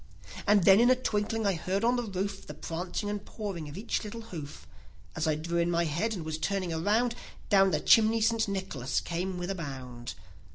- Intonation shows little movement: No, average, 4.5 semitones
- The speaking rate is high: Yes, fast, 210 wpm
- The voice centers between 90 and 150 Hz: No, high, 190 Hz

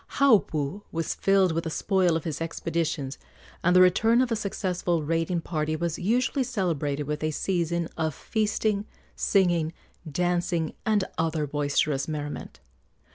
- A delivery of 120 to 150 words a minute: Yes, average, 140 wpm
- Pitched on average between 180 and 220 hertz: No, medium, 170 Hz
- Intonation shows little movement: No, average, 3.7 semitones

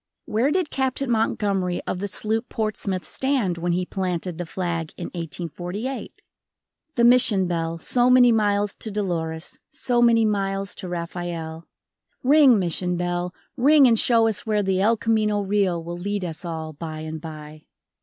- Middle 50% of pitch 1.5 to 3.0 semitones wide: No, average, 4.6 semitones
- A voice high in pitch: Yes, high, 195 Hz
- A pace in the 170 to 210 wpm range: No, average, 160 wpm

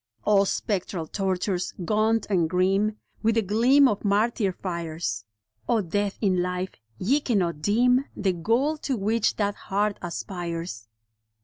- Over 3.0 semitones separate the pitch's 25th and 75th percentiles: Yes, average, 3.8 semitones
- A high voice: Yes, high, 200 Hz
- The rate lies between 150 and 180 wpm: No, average, 140 wpm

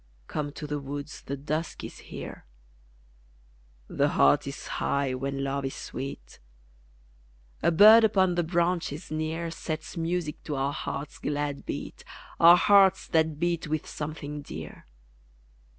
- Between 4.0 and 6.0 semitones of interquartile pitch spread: No, average, 3.1 semitones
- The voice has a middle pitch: Yes, medium, 155 Hz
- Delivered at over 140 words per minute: No, slow, 135 wpm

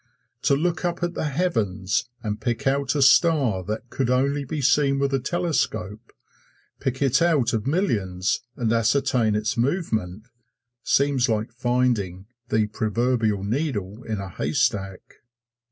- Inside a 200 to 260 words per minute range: No, average, 140 wpm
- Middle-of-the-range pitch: No, low, 125 Hz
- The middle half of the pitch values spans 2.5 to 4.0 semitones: No, average, 4.7 semitones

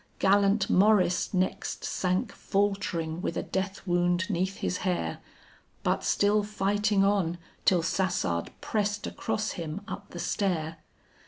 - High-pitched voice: Yes, high, 195 Hz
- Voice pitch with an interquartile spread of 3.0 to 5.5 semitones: No, narrow, 2.5 semitones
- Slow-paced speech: Yes, slow, 130 wpm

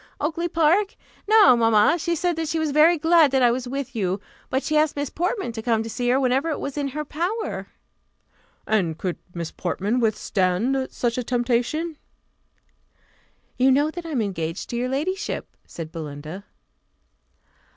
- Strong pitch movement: Yes, wide, 6.0 semitones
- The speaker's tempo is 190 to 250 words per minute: No, average, 170 wpm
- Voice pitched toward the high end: Yes, very high, 265 Hz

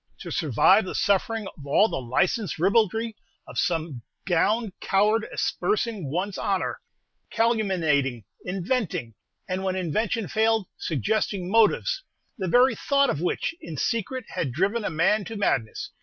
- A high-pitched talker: Yes, high, 195 Hz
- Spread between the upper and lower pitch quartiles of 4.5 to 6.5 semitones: Yes, average, 5.1 semitones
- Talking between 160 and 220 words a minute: No, average, 140 wpm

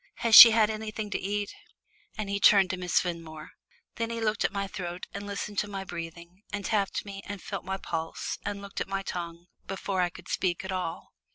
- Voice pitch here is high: Yes, high, 195 Hz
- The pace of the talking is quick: Yes, fast, 215 wpm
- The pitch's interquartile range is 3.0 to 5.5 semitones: No, narrow, 2.5 semitones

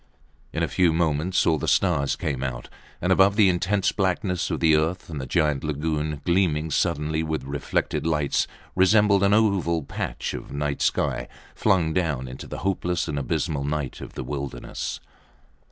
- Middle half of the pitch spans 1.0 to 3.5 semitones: No, average, 4.0 semitones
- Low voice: Yes, very low, 80 Hz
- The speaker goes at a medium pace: Yes, average, 165 wpm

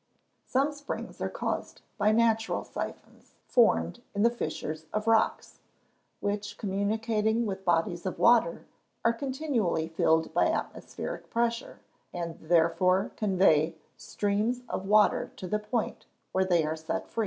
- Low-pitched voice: No, high, 205 Hz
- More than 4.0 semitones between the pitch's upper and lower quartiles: Yes, average, 4.7 semitones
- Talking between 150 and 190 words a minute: No, average, 140 wpm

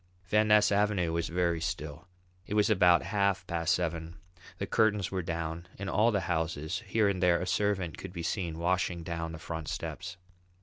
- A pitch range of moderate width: Yes, average, 3.1 semitones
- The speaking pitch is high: No, very low, 90 Hz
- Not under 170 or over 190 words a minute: Yes, average, 185 wpm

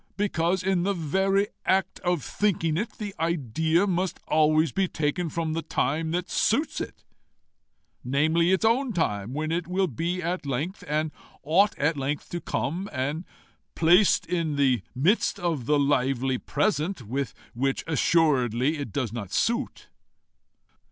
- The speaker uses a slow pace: No, average, 150 wpm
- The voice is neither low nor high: Yes, medium, 160 Hz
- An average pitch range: Yes, average, 4.5 semitones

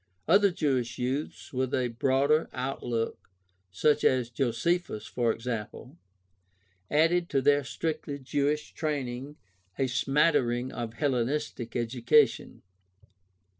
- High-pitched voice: No, low, 130 Hz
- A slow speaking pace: Yes, slow, 100 wpm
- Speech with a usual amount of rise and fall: Yes, average, 3.5 semitones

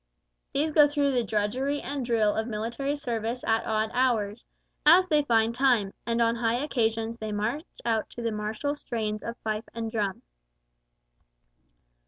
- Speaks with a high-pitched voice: Yes, high, 230 Hz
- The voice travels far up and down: No, average, 3.6 semitones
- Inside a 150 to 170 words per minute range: Yes, average, 160 wpm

